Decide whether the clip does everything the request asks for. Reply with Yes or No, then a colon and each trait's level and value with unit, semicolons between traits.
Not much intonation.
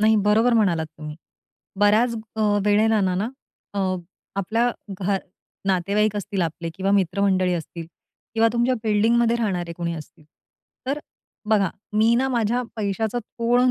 No: average, 3.6 semitones